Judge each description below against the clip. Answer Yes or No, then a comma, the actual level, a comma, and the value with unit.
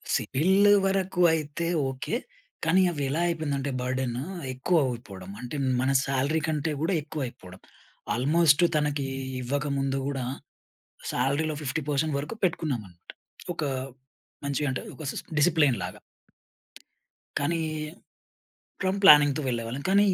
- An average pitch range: Yes, average, 3.5 semitones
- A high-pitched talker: No, medium, 145 Hz